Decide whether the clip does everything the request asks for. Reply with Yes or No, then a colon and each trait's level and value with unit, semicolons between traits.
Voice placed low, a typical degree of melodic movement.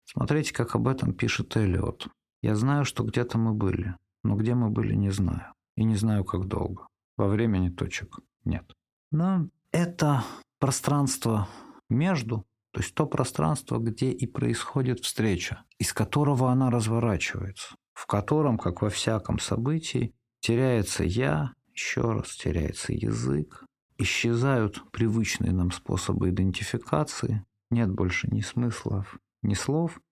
Yes: low, 115 Hz; average, 4.6 semitones